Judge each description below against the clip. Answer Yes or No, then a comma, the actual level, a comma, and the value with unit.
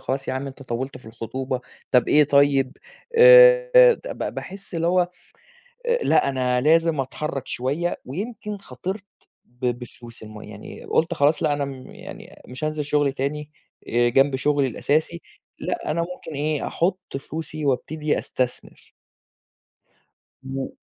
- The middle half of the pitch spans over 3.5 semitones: Yes, average, 4.1 semitones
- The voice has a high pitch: No, medium, 145 Hz